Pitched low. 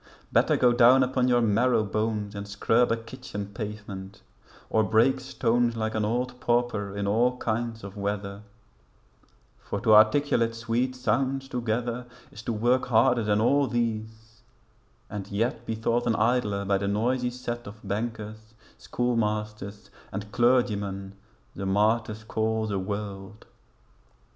Yes: low, 110 Hz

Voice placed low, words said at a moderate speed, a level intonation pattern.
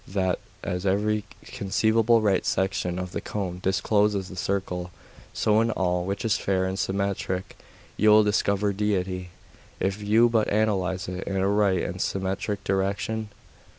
Yes: low, 100 Hz; average, 150 wpm; narrow, 2.1 semitones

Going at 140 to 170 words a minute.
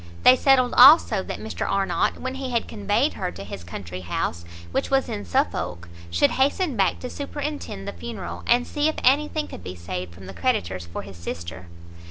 No: average, 195 wpm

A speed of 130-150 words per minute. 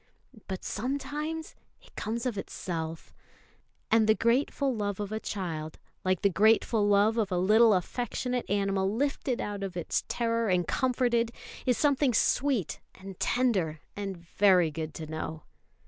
Yes: average, 145 wpm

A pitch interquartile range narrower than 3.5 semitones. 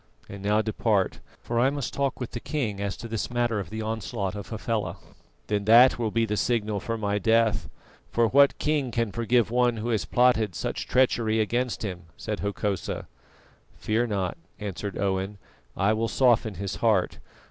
Yes: average, 2.7 semitones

